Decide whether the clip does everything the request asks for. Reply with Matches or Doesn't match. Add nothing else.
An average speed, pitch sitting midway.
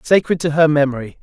Matches